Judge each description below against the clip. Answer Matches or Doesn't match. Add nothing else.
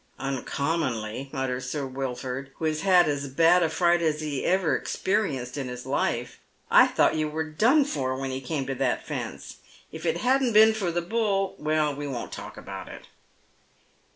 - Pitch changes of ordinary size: Matches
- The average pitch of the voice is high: Doesn't match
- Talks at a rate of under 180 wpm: Doesn't match